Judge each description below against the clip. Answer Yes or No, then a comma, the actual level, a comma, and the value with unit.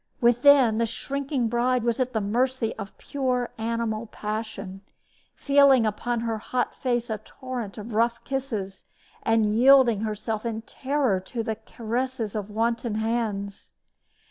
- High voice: Yes, high, 230 Hz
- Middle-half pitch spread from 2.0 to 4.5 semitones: Yes, average, 2.7 semitones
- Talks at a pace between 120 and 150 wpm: Yes, average, 140 wpm